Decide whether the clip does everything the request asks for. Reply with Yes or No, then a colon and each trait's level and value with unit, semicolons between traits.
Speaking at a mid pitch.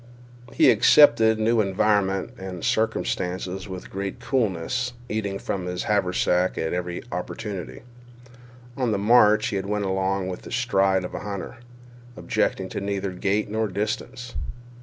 No: low, 100 Hz